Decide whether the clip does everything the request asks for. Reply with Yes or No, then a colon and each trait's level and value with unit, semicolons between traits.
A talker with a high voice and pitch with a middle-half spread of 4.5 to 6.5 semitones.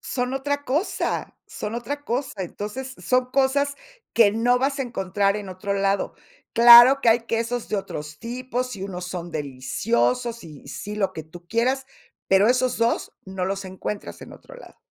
Yes: high, 230 Hz; average, 4.8 semitones